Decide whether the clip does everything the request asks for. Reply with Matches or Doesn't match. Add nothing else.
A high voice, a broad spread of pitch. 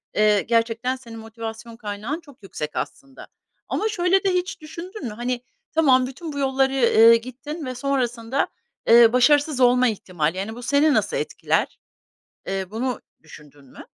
Doesn't match